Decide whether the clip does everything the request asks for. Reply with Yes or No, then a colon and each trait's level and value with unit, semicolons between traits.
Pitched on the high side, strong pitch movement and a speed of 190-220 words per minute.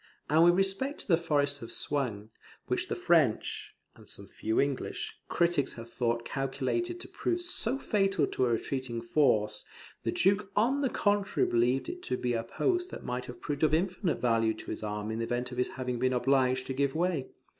No: low, 135 Hz; wide, 7.8 semitones; average, 200 wpm